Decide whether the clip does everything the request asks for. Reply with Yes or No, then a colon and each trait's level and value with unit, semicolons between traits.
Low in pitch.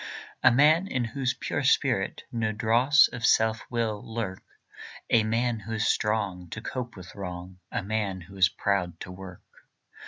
Yes: low, 110 Hz